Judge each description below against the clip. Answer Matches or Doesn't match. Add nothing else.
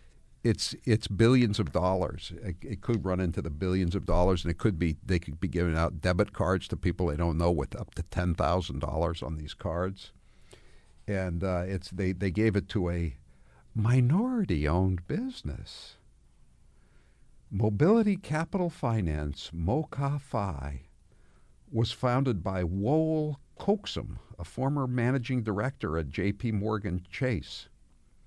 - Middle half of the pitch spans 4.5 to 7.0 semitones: Matches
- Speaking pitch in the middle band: Doesn't match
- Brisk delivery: Doesn't match